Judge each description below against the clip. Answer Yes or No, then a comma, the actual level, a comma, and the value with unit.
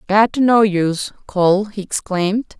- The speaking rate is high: No, average, 160 wpm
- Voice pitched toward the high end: Yes, high, 200 Hz